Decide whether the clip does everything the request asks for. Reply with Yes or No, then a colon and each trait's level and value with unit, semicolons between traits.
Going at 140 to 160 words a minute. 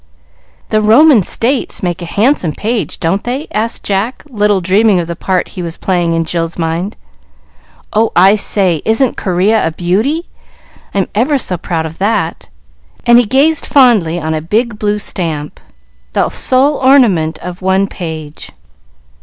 Yes: average, 155 wpm